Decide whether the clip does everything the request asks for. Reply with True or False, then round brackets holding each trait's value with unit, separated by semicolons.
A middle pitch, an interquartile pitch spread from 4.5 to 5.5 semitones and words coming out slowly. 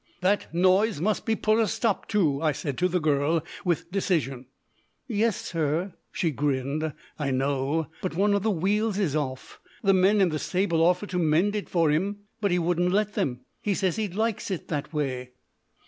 False (175 Hz; 5.1 semitones; 195 wpm)